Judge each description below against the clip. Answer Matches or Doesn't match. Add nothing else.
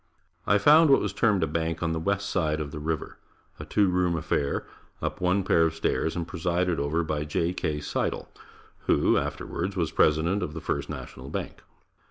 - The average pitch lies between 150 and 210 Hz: Doesn't match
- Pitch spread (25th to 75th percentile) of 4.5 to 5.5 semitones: Doesn't match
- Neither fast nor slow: Matches